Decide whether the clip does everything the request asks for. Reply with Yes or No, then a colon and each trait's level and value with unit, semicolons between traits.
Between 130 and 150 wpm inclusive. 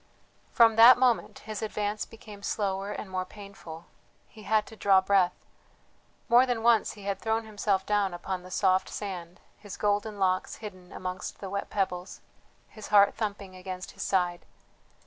No: average, 165 wpm